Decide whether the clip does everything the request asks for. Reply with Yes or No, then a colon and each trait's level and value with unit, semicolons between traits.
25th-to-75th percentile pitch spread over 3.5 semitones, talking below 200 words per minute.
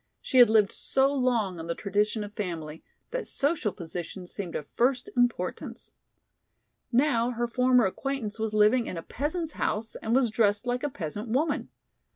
Yes: average, 4.0 semitones; average, 170 wpm